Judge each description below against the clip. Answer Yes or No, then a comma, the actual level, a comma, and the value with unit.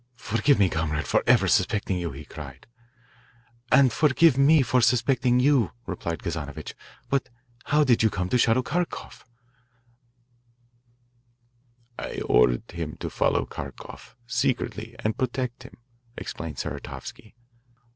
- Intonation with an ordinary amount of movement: No, wide, 7.8 semitones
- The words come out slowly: Yes, slow, 125 wpm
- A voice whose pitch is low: Yes, low, 115 Hz